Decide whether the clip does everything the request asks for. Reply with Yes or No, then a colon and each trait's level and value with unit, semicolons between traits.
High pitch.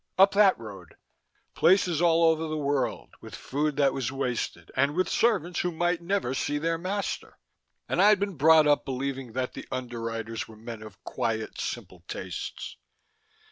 No: medium, 145 Hz